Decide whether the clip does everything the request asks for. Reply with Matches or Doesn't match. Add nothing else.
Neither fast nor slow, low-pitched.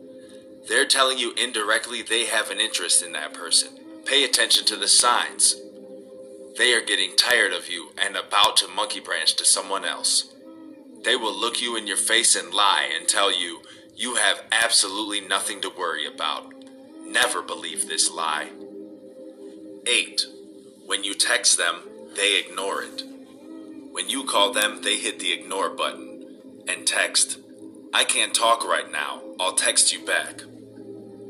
Matches